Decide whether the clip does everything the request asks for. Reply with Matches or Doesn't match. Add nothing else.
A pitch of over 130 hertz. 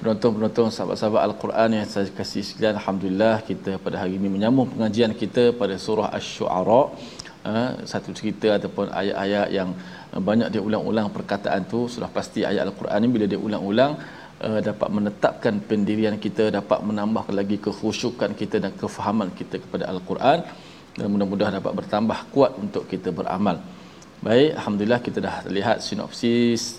Doesn't match